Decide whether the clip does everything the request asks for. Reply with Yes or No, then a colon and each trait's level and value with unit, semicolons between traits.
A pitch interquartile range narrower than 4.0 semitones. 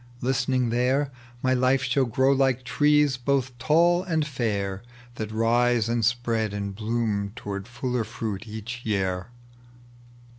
Yes: average, 3.4 semitones